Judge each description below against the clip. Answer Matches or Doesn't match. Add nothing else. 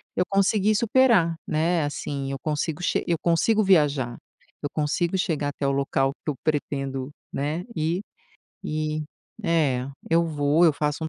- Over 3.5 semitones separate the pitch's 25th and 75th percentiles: Doesn't match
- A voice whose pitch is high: Doesn't match